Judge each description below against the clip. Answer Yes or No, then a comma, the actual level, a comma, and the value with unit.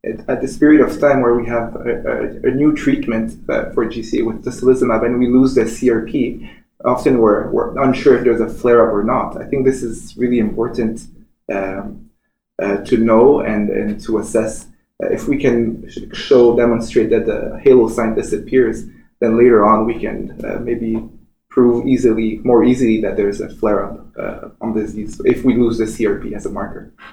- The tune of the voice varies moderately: No, narrow, 1.8 semitones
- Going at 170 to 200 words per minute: Yes, average, 190 wpm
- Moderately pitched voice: No, low, 115 Hz